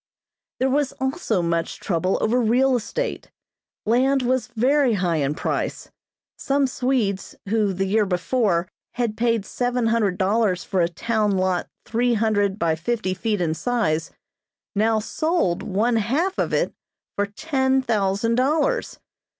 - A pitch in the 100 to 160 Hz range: No, high, 225 Hz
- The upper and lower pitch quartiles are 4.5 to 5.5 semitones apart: Yes, average, 4.8 semitones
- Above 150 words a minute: No, average, 140 wpm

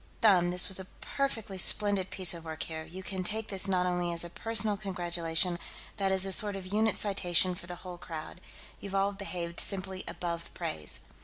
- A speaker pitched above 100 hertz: Yes, medium, 185 Hz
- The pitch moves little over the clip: Yes, narrow, 2.3 semitones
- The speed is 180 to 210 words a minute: Yes, average, 200 wpm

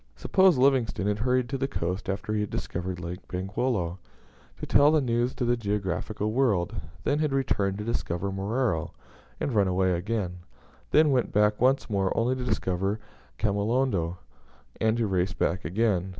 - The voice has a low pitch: Yes, low, 105 Hz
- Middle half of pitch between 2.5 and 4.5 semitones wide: No, average, 5.0 semitones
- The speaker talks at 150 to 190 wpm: Yes, average, 165 wpm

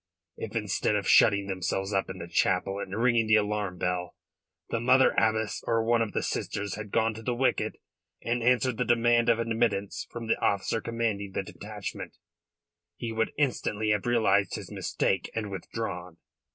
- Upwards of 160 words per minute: Yes, average, 175 wpm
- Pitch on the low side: Yes, low, 110 Hz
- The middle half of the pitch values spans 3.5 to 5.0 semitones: No, average, 2.7 semitones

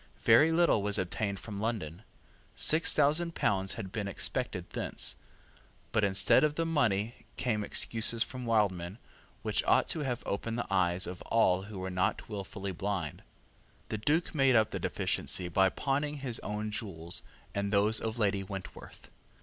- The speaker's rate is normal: Yes, average, 160 wpm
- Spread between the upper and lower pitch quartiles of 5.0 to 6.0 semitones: No, average, 3.9 semitones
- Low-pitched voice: Yes, low, 105 Hz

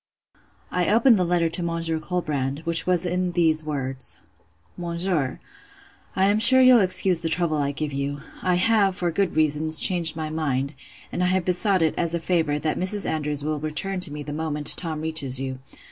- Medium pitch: Yes, medium, 165 Hz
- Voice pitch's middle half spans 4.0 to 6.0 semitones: No, average, 3.3 semitones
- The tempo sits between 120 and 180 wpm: No, average, 190 wpm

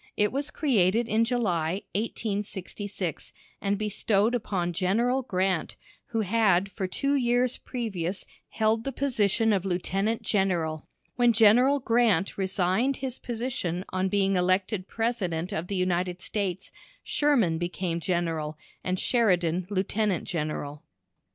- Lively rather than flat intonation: No, average, 4.2 semitones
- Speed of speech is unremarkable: No, slow, 125 wpm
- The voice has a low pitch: No, high, 195 Hz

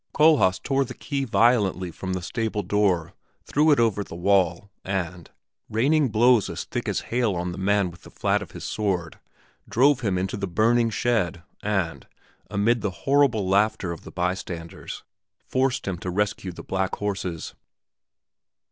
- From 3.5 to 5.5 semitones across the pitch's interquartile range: Yes, average, 4.5 semitones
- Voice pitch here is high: No, low, 100 Hz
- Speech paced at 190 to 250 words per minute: No, average, 165 wpm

